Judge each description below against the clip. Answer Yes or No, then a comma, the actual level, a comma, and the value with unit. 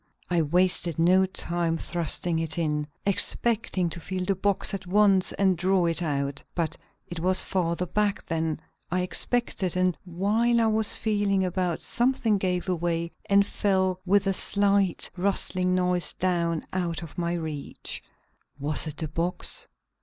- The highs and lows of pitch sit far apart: No, average, 2.7 semitones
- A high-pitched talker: No, medium, 180 Hz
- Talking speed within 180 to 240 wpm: No, average, 155 wpm